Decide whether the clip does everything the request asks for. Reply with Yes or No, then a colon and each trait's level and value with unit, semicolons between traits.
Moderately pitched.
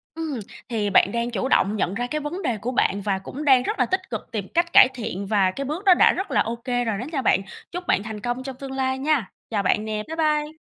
No: high, 245 Hz